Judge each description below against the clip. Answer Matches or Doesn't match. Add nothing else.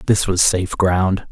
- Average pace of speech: Matches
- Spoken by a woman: Doesn't match